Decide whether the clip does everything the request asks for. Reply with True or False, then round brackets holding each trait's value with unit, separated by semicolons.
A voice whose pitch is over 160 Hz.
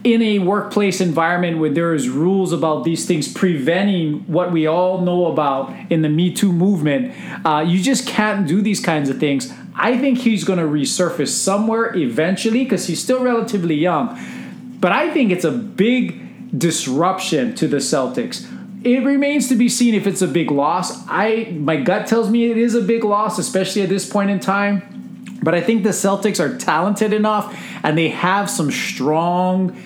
True (190 Hz)